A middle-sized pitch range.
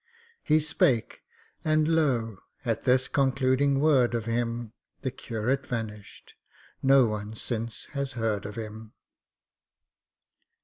Yes: average, 3.5 semitones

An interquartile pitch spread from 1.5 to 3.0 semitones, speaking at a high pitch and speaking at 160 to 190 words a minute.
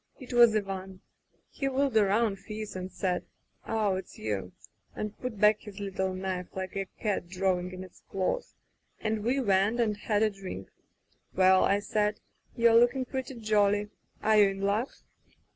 Yes: narrow, 2.6 semitones; high, 205 Hz; average, 165 wpm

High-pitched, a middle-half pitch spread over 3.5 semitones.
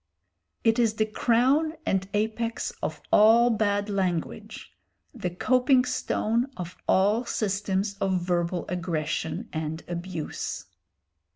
Yes: high, 200 Hz; average, 4.4 semitones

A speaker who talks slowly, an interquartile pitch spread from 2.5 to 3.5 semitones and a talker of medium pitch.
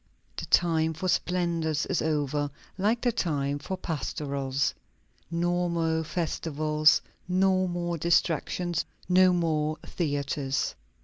Yes: slow, 110 wpm; average, 2.8 semitones; medium, 165 Hz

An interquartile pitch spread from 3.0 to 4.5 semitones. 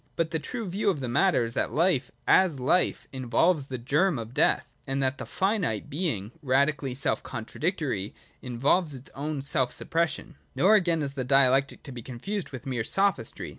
No: average, 5.2 semitones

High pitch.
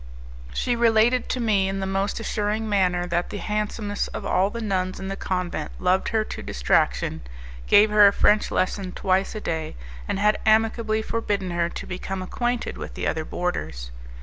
Yes: high, 200 Hz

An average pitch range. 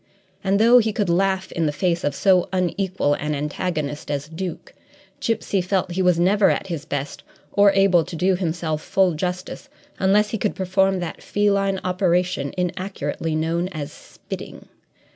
Yes: average, 3.0 semitones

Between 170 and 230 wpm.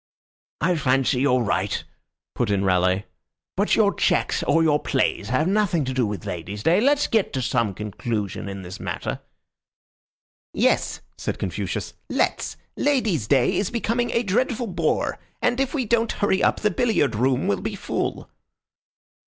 No: average, 160 wpm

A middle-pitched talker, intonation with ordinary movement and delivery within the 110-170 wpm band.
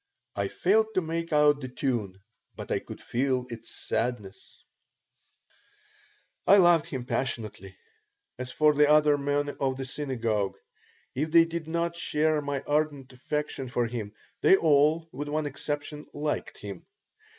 Yes: medium, 145 Hz; average, 3.7 semitones; average, 145 wpm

